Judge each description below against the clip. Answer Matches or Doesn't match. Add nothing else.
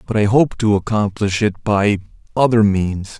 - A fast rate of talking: Doesn't match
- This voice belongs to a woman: Doesn't match